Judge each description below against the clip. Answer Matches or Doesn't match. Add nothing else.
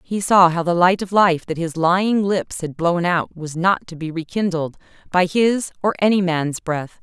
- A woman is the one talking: Matches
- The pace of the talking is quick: Matches